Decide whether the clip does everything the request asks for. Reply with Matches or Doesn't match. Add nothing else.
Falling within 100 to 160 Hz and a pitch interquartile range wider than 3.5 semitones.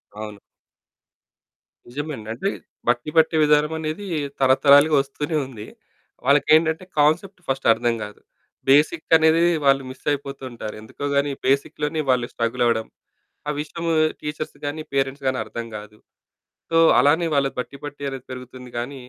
Doesn't match